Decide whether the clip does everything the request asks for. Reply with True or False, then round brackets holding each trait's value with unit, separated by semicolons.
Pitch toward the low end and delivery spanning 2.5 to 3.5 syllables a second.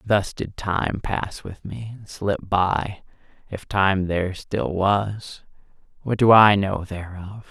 True (100 Hz; 3.4 syllables/s)